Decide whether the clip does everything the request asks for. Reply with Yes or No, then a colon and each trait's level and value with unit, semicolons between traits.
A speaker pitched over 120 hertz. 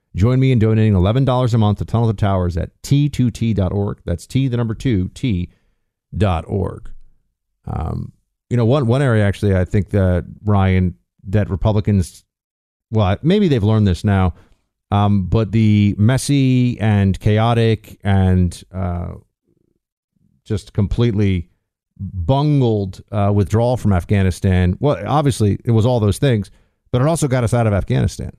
No: low, 105 Hz